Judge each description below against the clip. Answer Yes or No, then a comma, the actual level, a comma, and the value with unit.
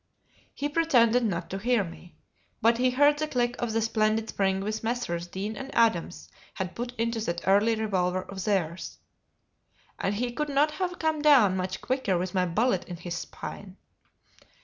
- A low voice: No, high, 220 Hz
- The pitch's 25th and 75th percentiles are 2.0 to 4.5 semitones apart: No, average, 4.9 semitones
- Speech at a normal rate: Yes, average, 175 wpm